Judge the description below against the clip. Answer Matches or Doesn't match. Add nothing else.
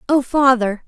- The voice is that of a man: Doesn't match